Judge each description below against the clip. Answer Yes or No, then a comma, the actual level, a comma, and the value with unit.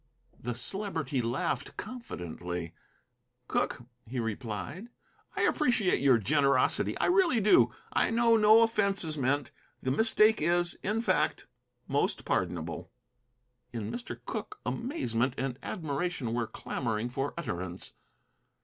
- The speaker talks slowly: Yes, slow, 120 wpm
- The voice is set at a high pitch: No, medium, 140 Hz